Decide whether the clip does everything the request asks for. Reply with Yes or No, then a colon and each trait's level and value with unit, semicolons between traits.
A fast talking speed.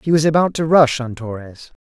Yes: fast, 225 wpm